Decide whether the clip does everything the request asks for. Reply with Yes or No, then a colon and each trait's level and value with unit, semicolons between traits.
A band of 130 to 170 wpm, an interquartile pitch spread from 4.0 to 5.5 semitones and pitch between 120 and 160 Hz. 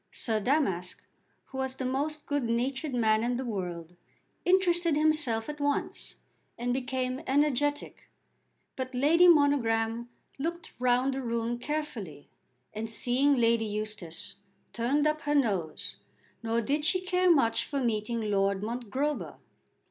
No: slow, 135 wpm; average, 4.4 semitones; very high, 255 Hz